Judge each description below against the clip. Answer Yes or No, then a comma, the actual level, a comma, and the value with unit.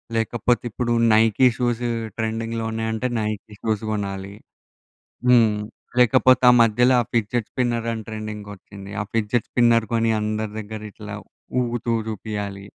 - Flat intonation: Yes, narrow, 1.9 semitones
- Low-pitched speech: Yes, low, 110 Hz